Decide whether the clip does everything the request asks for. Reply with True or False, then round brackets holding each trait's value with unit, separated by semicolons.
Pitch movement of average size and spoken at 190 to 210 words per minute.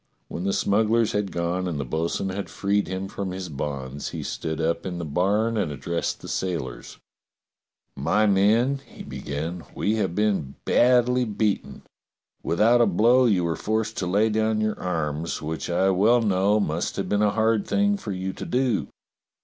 False (4.4 semitones; 180 wpm)